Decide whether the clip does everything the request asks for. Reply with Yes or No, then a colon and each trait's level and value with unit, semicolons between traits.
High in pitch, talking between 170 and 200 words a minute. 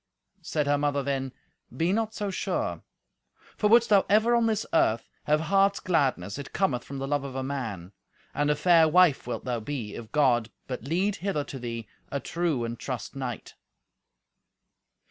No: medium, 145 Hz; average, 180 wpm